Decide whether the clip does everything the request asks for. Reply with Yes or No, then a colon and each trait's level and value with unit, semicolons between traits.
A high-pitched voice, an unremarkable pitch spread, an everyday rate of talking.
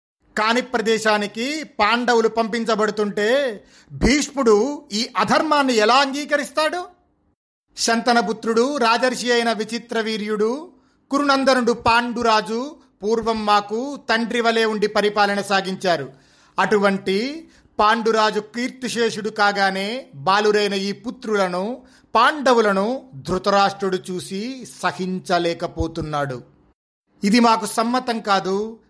Yes: high, 225 Hz; average, 3.4 semitones; average, 80 wpm